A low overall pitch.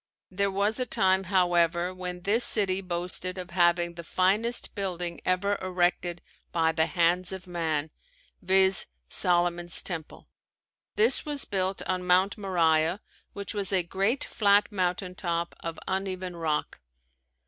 No: medium, 185 Hz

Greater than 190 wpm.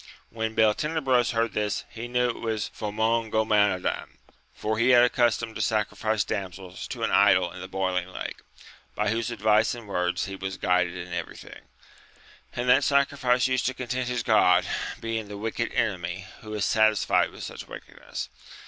No: average, 165 wpm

